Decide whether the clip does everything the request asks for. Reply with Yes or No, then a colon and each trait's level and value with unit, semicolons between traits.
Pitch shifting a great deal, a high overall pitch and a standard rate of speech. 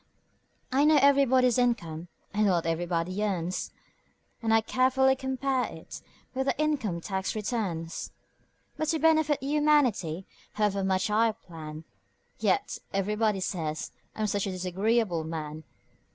No: wide, 6.8 semitones; high, 210 Hz; slow, 125 wpm